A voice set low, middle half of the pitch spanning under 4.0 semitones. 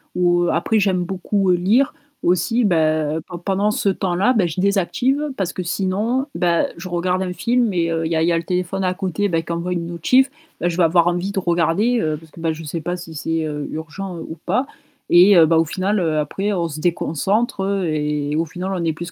No: medium, 175 Hz; average, 2.9 semitones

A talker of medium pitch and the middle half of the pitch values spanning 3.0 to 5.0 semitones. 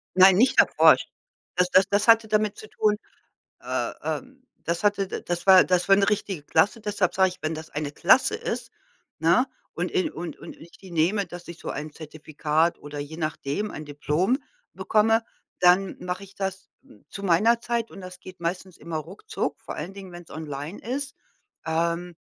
Yes: medium, 180 Hz; average, 3.8 semitones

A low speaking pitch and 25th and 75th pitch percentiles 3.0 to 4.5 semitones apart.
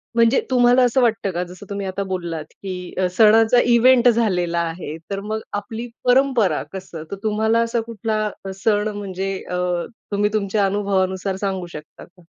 No: high, 205 Hz; average, 3.3 semitones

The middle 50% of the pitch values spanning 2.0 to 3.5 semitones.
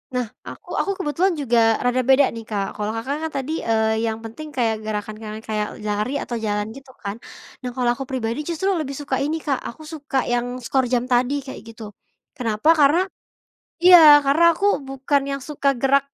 No: average, 4.2 semitones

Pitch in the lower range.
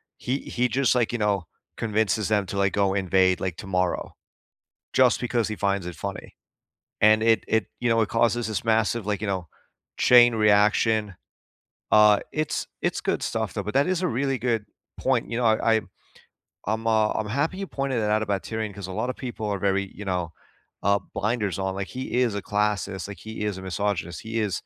Yes: low, 105 Hz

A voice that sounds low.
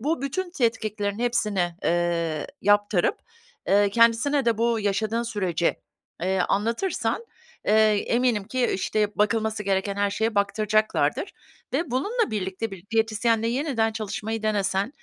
No: high, 215 Hz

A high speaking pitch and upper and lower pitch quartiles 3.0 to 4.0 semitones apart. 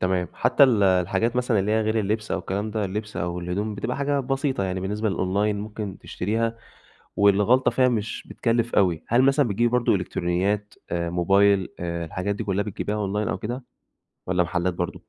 No: low, 105 Hz; average, 3.5 semitones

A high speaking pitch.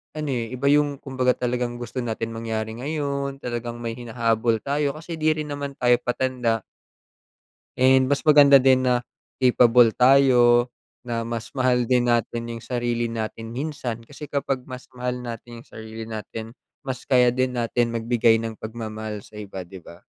No: low, 120 Hz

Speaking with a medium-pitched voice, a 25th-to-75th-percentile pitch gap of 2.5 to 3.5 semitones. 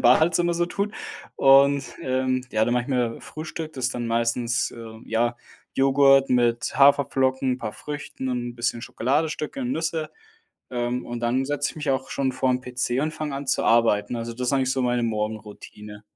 No: low, 130 Hz; average, 2.9 semitones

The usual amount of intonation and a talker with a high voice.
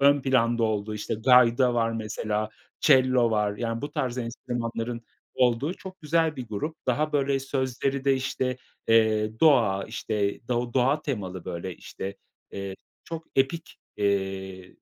No: average, 4.1 semitones; low, 120 Hz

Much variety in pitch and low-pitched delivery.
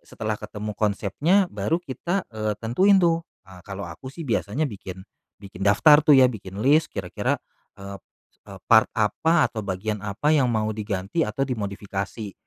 Yes: wide, 6.8 semitones; low, 110 Hz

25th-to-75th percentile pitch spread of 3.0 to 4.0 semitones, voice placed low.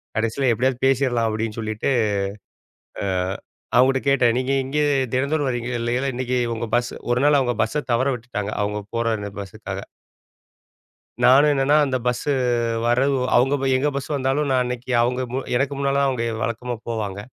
No: narrow, 2.5 semitones; low, 125 Hz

